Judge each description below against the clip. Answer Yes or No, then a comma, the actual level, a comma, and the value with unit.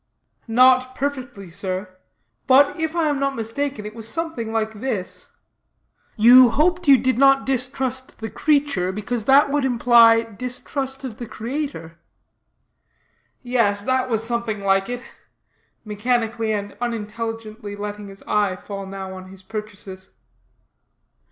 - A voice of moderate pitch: No, high, 230 Hz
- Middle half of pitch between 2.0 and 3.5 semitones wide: No, average, 3.9 semitones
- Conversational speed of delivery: No, slow, 130 wpm